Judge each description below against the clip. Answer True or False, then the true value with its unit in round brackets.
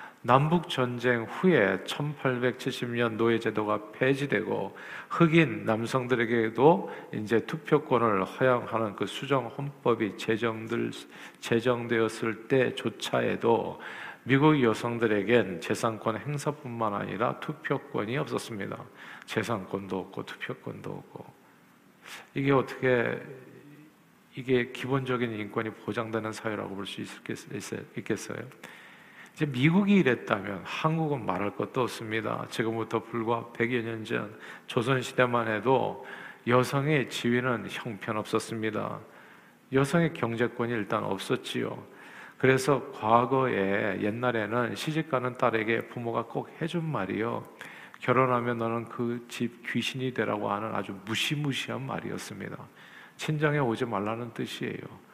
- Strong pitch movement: False (2.9 semitones)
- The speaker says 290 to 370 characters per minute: False (270 characters per minute)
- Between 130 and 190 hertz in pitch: False (120 Hz)